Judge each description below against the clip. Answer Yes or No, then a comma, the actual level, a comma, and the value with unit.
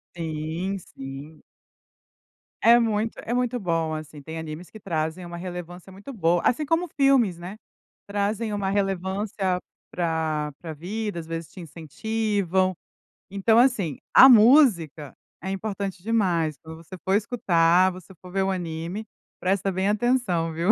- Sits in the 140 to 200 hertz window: Yes, medium, 185 Hz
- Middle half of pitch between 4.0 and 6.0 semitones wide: Yes, average, 4.3 semitones